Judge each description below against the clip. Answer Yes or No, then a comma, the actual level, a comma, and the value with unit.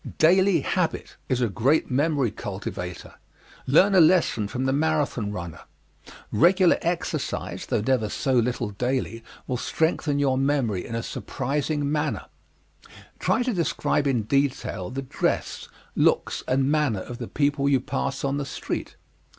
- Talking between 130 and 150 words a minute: Yes, average, 145 wpm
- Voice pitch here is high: No, low, 135 Hz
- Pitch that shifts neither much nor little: Yes, average, 4.2 semitones